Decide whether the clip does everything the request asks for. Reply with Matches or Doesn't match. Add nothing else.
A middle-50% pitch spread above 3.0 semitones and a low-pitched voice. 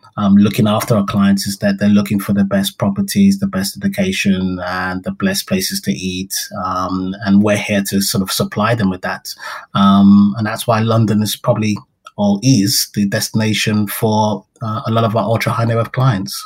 Doesn't match